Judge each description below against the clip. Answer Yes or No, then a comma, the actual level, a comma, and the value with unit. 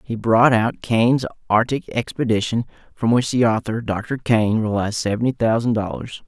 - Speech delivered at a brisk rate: No, average, 155 wpm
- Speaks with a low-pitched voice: Yes, low, 115 Hz